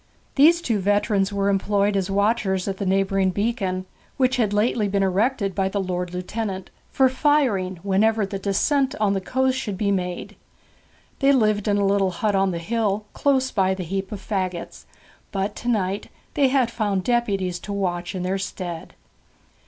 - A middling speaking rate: Yes, average, 175 wpm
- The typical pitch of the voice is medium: No, high, 200 Hz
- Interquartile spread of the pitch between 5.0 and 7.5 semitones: No, average, 2.9 semitones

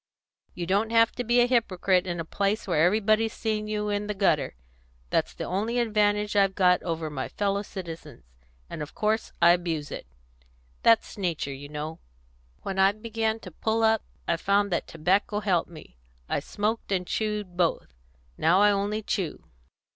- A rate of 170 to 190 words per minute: Yes, average, 175 wpm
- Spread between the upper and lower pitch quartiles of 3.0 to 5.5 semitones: Yes, average, 3.7 semitones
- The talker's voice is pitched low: No, high, 200 Hz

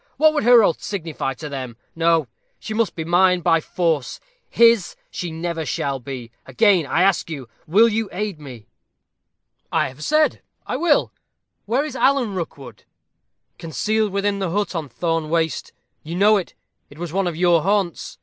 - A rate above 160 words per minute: Yes, average, 170 wpm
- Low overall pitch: No, medium, 175 Hz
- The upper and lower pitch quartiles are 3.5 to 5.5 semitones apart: Yes, average, 5.0 semitones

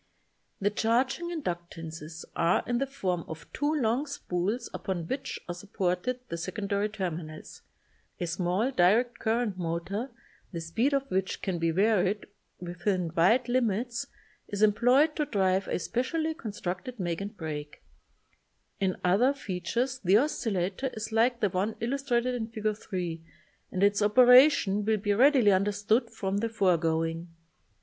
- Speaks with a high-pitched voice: Yes, high, 205 Hz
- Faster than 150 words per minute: No, average, 140 wpm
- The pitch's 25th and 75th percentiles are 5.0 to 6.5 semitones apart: Yes, average, 5.3 semitones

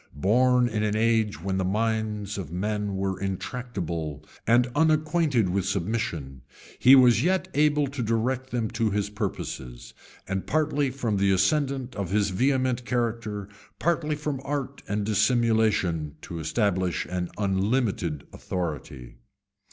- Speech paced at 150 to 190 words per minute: No, slow, 135 wpm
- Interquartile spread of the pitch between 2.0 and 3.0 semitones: No, average, 5.1 semitones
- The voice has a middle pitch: No, low, 110 Hz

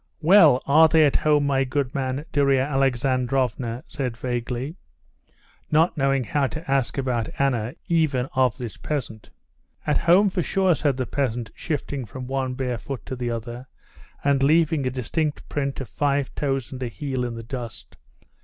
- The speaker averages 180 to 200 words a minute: No, average, 170 wpm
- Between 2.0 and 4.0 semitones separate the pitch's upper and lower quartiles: Yes, average, 2.7 semitones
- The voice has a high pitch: No, low, 135 Hz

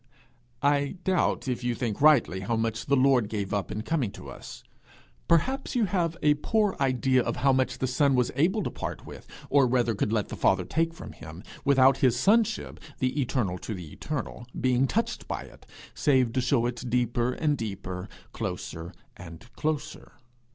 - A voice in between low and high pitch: No, low, 130 Hz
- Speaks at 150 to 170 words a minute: No, average, 185 wpm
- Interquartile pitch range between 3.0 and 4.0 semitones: No, average, 4.5 semitones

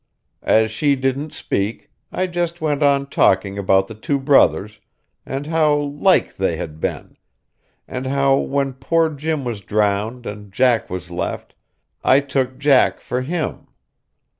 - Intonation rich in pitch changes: Yes, wide, 5.7 semitones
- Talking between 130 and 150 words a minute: Yes, average, 145 wpm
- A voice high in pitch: No, low, 135 Hz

